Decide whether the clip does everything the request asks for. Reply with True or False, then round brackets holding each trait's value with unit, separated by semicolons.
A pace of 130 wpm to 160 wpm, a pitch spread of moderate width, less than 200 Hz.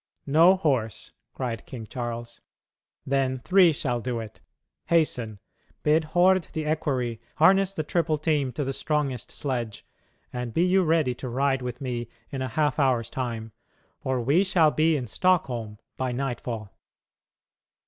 True (150 wpm; 4.6 semitones; 135 Hz)